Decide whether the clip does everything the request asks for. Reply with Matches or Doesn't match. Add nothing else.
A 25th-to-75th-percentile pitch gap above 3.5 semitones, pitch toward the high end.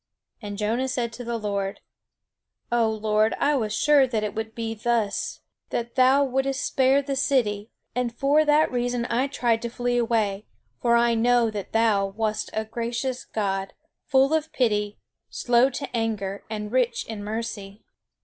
Doesn't match